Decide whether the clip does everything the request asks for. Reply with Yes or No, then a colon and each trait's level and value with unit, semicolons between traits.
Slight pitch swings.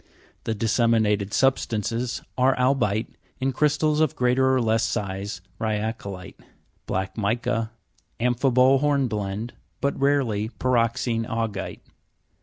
No: average, 3.6 semitones